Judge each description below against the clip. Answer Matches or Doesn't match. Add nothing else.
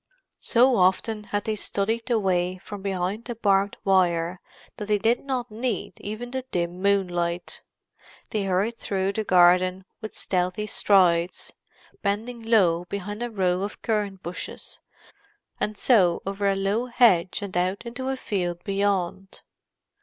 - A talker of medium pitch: Doesn't match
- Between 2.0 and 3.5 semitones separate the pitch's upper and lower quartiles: Matches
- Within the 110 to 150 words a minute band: Matches